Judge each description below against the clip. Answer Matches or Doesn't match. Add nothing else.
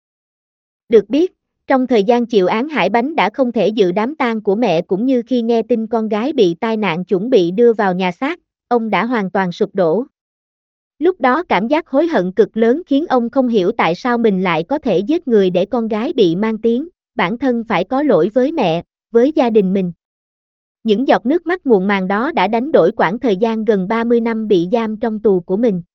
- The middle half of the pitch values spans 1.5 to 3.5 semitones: Doesn't match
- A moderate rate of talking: Matches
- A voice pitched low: Doesn't match